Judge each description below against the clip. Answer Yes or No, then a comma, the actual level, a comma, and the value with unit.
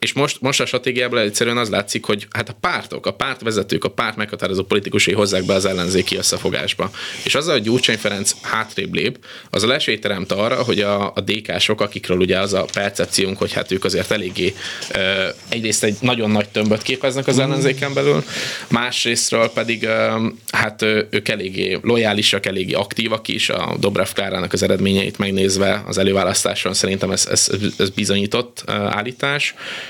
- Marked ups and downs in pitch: No, average, 3.8 semitones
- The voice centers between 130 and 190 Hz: No, low, 110 Hz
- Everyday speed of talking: No, fast, 160 wpm